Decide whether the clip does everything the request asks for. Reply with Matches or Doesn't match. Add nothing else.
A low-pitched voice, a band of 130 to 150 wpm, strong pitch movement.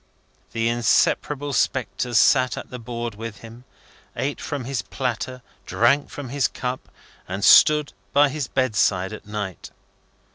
Doesn't match